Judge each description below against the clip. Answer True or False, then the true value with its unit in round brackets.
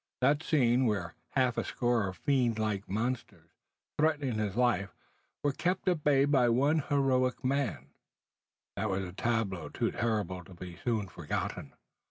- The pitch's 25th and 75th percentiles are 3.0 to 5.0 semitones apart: False (5.6 semitones)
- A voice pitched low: True (120 Hz)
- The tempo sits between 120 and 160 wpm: True (155 wpm)